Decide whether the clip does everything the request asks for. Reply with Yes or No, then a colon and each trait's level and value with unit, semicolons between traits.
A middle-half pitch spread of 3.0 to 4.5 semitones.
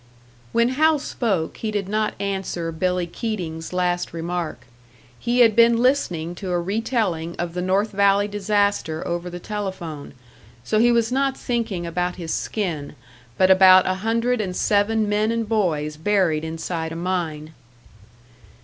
Yes: average, 4.2 semitones